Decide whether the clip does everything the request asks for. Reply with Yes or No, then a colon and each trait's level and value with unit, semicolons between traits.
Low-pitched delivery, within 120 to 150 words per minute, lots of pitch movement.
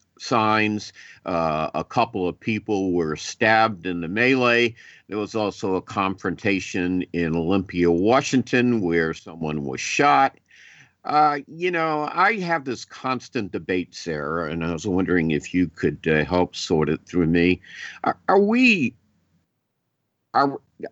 Yes: very low, 95 Hz; average, 140 wpm; wide, 5.9 semitones